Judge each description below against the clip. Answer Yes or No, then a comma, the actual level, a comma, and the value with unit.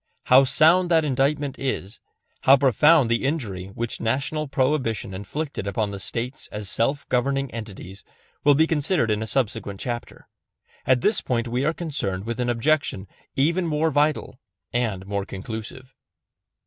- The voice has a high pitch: No, low, 130 Hz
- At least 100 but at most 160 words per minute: Yes, average, 150 wpm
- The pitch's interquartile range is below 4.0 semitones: No, average, 4.9 semitones